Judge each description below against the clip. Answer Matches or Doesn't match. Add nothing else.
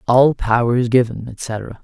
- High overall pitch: Doesn't match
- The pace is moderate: Matches